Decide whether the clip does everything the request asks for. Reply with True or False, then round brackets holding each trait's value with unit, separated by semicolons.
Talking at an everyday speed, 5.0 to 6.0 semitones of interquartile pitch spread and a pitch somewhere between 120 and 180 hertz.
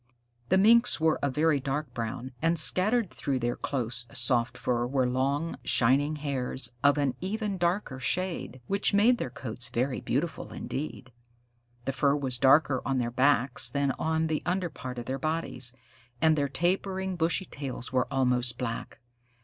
False (165 wpm; 4.6 semitones; 140 Hz)